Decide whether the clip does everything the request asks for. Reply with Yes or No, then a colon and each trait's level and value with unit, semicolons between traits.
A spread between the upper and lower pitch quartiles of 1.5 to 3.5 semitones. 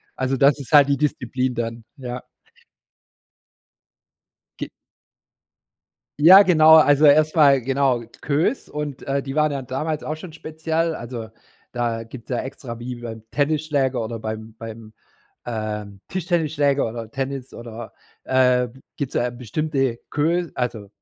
No: average, 4.2 semitones